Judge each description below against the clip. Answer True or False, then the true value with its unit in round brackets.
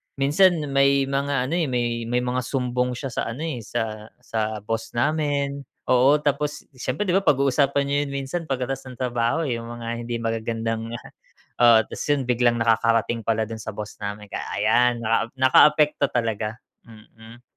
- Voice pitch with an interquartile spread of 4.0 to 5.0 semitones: False (3.4 semitones)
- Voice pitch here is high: False (125 Hz)